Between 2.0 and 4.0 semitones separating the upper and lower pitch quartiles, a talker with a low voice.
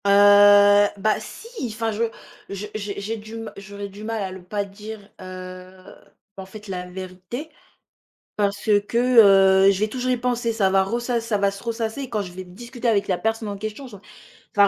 No: narrow, 2.5 semitones; high, 205 Hz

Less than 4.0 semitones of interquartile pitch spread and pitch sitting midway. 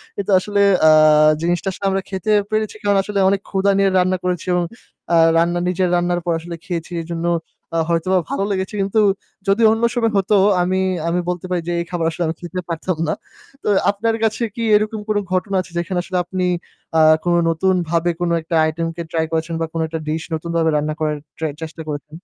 Yes: average, 2.8 semitones; medium, 180 Hz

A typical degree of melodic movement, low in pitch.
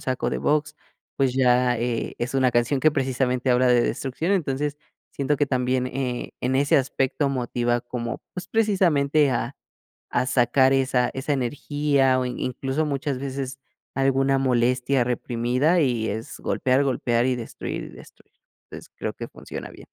No: narrow, 2.1 semitones; low, 130 Hz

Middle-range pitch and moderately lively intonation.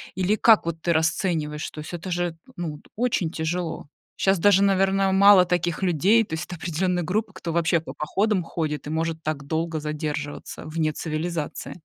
Yes: medium, 170 Hz; average, 3.1 semitones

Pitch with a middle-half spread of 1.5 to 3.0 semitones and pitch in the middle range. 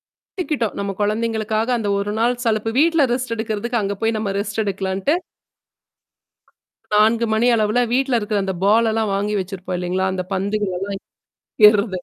No: narrow, 2.5 semitones; high, 215 Hz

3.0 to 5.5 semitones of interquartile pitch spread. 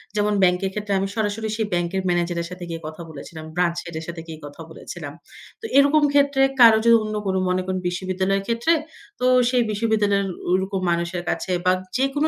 Yes: average, 4.0 semitones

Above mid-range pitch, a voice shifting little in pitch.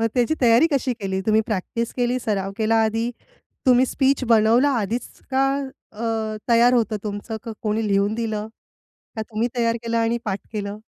Yes: high, 225 Hz; narrow, 2.2 semitones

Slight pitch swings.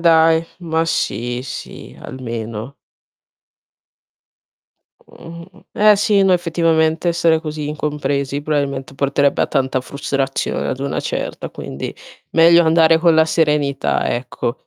No: average, 3.4 semitones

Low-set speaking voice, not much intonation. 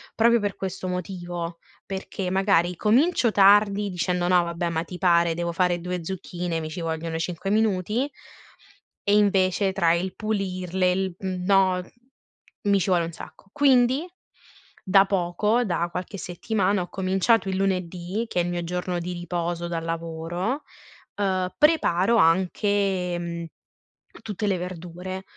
No: medium, 185 Hz; narrow, 2.3 semitones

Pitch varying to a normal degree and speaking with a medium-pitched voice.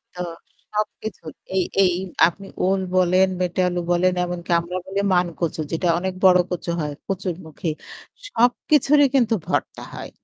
No: narrow, 2.0 semitones; medium, 180 Hz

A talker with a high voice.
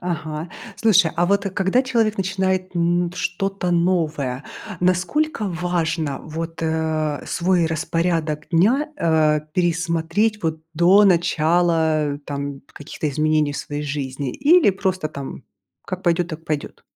No: medium, 170 Hz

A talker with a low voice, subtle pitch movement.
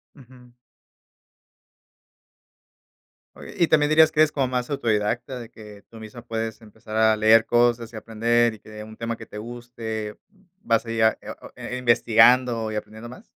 Yes: low, 115 Hz; narrow, 2.1 semitones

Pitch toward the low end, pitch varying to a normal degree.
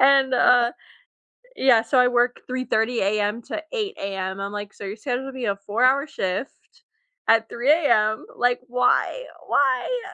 No: high, 245 Hz; average, 3.8 semitones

